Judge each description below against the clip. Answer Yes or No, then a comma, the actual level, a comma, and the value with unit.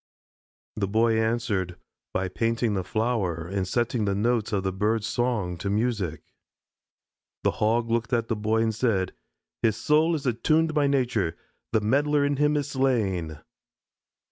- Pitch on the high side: No, low, 110 Hz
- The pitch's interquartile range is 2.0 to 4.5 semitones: Yes, average, 3.9 semitones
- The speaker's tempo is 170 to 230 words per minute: No, average, 155 wpm